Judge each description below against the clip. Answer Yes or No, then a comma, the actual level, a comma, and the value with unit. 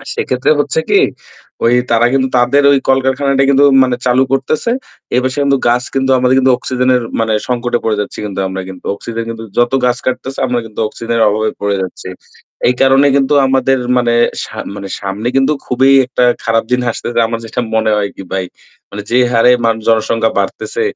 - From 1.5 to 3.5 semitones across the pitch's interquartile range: Yes, average, 2.9 semitones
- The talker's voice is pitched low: Yes, low, 125 Hz